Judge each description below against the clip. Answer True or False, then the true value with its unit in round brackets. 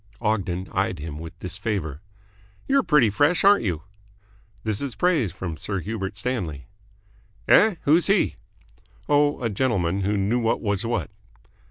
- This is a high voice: False (105 Hz)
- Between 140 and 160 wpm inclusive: True (145 wpm)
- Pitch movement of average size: False (6.2 semitones)